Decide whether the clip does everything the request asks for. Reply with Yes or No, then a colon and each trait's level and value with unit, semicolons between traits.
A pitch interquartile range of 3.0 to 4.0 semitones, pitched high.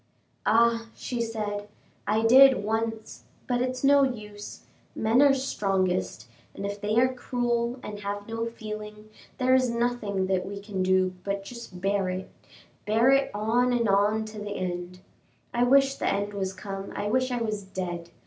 Yes: average, 3.3 semitones; high, 215 Hz